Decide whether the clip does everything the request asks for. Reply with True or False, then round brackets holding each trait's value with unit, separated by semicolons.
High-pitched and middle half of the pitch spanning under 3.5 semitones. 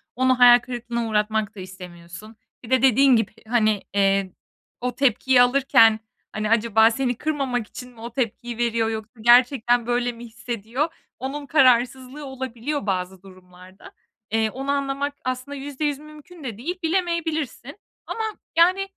False (245 Hz; 3.8 semitones)